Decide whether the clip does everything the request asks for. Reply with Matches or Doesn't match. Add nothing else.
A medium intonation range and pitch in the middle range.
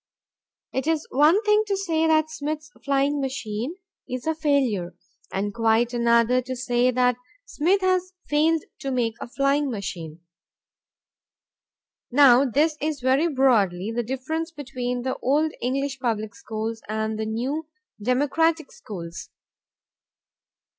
Doesn't match